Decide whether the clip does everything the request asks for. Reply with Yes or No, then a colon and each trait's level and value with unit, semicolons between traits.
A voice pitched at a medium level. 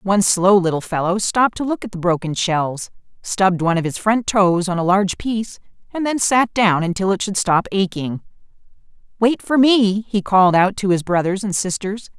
No: high, 195 Hz